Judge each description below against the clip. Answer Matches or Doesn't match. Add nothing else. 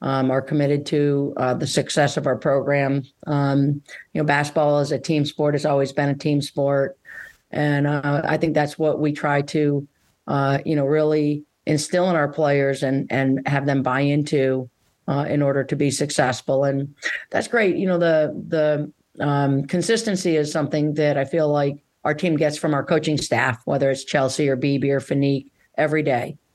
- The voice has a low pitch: Doesn't match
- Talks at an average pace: Matches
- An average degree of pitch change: Doesn't match